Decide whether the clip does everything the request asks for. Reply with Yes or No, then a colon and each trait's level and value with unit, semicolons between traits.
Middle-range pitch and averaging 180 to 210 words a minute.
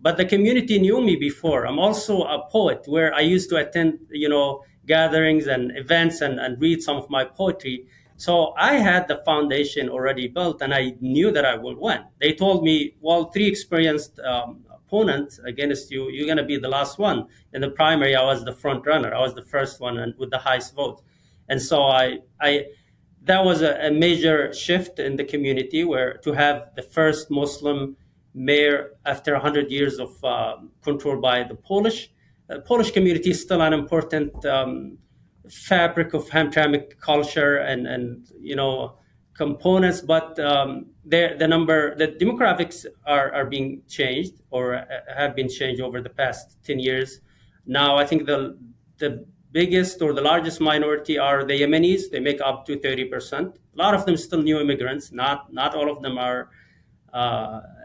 Yes: medium, 145 Hz; average, 185 wpm